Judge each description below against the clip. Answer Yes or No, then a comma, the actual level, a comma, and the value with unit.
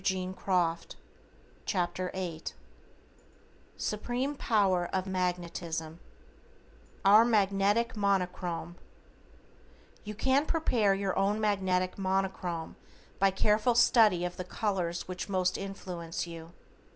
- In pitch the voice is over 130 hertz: Yes, high, 190 Hz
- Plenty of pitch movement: No, average, 2.9 semitones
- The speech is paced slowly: Yes, slow, 90 wpm